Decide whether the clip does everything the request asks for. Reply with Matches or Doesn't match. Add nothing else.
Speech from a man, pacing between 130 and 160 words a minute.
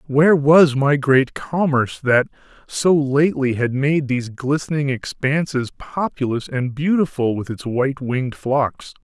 Matches